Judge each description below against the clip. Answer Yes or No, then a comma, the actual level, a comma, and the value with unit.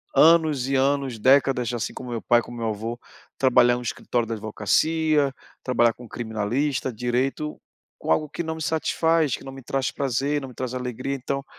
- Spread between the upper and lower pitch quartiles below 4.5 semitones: Yes, average, 3.0 semitones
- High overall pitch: No, low, 130 Hz